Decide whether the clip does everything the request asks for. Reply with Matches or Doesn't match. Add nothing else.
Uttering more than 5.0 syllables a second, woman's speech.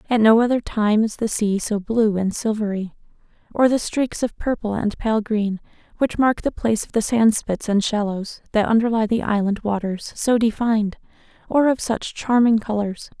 Doesn't match